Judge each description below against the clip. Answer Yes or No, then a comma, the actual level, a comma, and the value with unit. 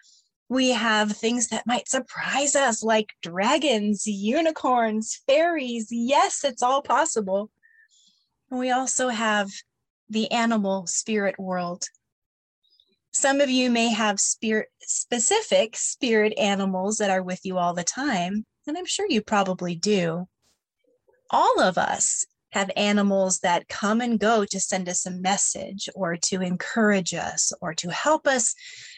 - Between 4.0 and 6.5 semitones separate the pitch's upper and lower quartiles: Yes, average, 5.1 semitones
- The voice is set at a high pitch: Yes, high, 220 Hz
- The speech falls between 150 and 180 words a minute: No, average, 140 wpm